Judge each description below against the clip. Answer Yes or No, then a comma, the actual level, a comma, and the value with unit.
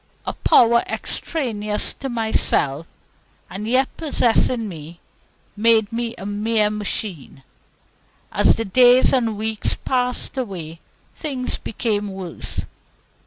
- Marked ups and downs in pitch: No, average, 3.3 semitones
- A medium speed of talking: No, slow, 110 wpm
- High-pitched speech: Yes, high, 220 Hz